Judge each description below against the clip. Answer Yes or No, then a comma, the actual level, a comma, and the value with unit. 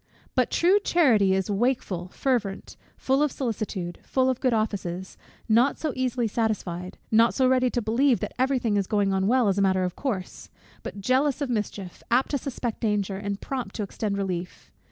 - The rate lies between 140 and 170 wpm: No, average, 190 wpm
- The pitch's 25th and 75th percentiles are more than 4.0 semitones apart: Yes, average, 4.8 semitones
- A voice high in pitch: Yes, high, 220 Hz